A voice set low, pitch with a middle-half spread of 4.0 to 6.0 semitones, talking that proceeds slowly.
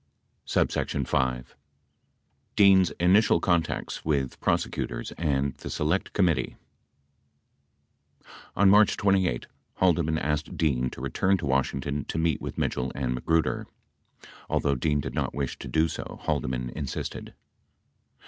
Yes: very low, 75 Hz; average, 4.6 semitones; slow, 120 wpm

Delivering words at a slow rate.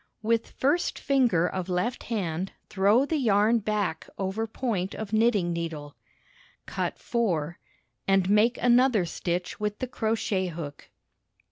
Yes: slow, 130 wpm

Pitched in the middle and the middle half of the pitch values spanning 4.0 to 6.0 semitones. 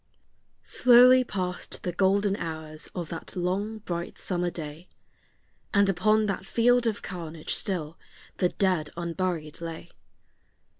No: medium, 180 Hz; average, 3.3 semitones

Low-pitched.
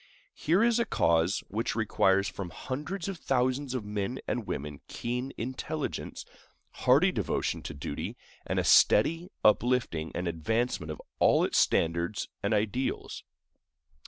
Yes: low, 110 Hz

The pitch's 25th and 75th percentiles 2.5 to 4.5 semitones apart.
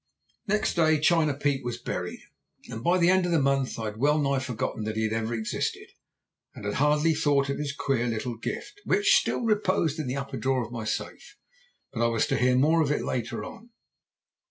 No: average, 5.1 semitones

